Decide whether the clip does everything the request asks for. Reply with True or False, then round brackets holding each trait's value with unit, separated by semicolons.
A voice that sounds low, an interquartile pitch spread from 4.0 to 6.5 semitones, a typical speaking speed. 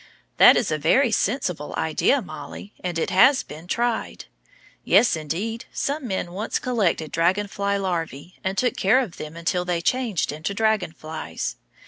False (190 Hz; 5.3 semitones; 160 wpm)